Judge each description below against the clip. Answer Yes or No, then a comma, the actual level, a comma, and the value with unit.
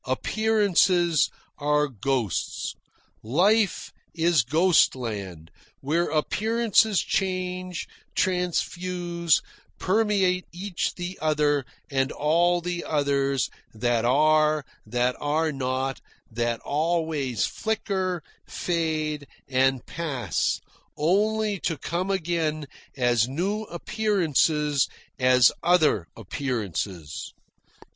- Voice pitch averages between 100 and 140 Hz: No, medium, 155 Hz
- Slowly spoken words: Yes, slow, 85 wpm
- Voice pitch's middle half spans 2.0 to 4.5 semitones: No, wide, 5.4 semitones